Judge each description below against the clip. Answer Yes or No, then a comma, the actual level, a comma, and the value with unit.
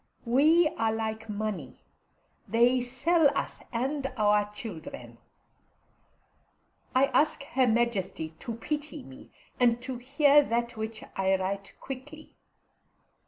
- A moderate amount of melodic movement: Yes, average, 4.3 semitones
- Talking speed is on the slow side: Yes, slow, 115 wpm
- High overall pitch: Yes, high, 235 Hz